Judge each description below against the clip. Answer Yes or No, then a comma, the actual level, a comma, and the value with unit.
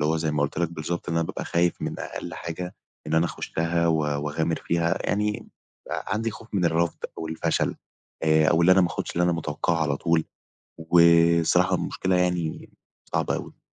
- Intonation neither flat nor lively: No, narrow, 1.4 semitones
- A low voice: Yes, very low, 85 Hz